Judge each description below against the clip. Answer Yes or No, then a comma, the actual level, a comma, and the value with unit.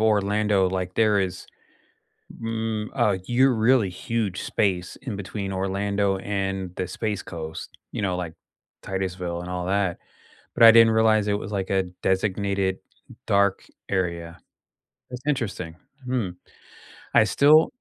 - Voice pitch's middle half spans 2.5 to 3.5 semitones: Yes, average, 2.9 semitones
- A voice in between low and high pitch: No, low, 100 Hz